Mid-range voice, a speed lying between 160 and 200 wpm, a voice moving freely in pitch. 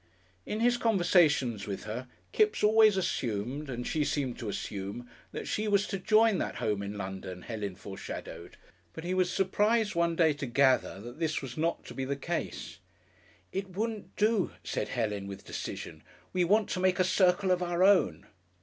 Yes: medium, 170 Hz; average, 180 wpm; wide, 8.6 semitones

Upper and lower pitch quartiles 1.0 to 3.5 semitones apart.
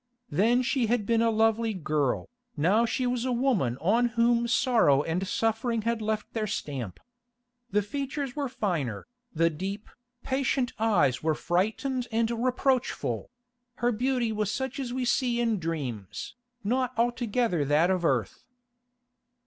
No: wide, 5.4 semitones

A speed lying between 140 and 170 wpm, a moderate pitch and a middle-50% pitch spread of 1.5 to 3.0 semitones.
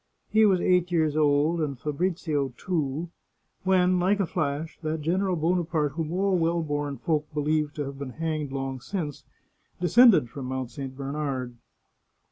No: average, 155 wpm; medium, 155 Hz; average, 3.8 semitones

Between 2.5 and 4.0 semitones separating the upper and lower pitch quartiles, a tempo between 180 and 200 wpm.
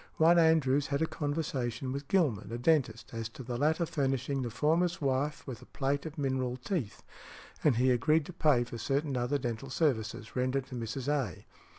Yes: average, 3.6 semitones; average, 190 wpm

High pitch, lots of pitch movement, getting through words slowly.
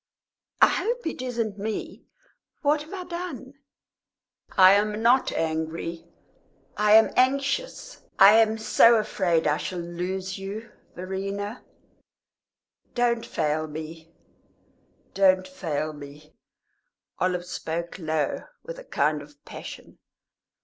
Yes: high, 195 Hz; wide, 6.3 semitones; slow, 115 wpm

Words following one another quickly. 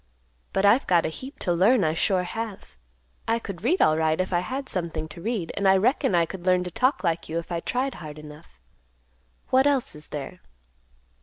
Yes: fast, 210 wpm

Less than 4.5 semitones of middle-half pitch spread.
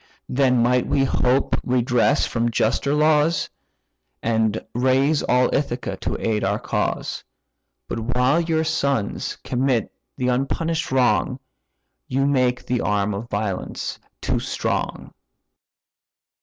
Yes: average, 3.0 semitones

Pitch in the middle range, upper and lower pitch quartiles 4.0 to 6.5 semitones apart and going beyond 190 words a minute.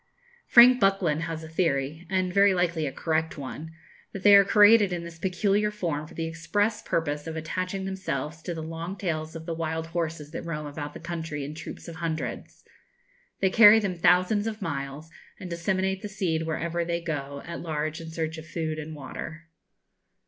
No: medium, 165 Hz; average, 3.0 semitones; average, 200 wpm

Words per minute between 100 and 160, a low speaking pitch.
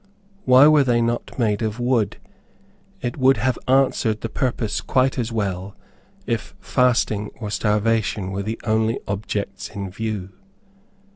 Yes: average, 140 wpm; low, 110 Hz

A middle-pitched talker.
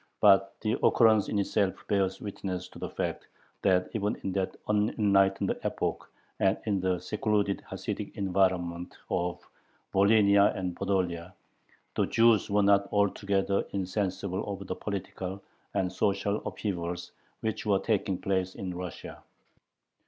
No: low, 100 Hz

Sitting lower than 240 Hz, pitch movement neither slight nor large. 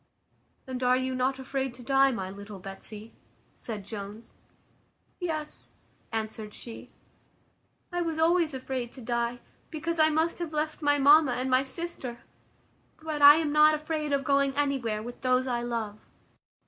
No: very high, 265 Hz; average, 4.3 semitones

